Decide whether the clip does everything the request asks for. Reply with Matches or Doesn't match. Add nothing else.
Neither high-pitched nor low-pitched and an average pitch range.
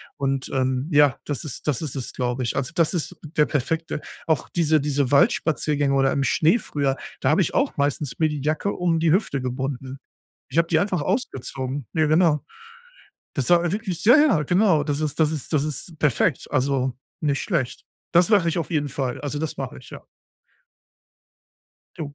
Matches